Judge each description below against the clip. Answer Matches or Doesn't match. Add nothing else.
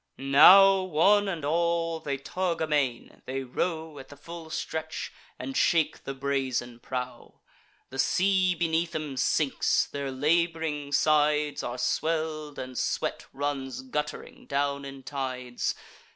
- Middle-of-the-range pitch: Matches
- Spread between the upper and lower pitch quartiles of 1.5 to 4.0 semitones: Matches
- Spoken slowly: Matches